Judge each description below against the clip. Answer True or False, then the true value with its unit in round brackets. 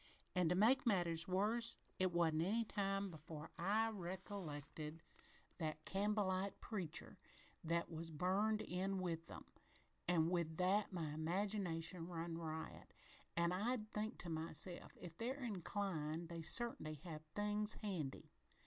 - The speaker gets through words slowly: True (130 wpm)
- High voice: False (180 Hz)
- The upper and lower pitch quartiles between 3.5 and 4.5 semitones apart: True (4.0 semitones)